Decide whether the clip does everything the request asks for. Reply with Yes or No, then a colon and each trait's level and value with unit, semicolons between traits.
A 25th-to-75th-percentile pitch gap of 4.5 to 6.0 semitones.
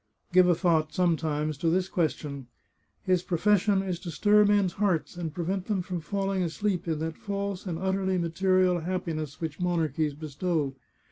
No: average, 3.0 semitones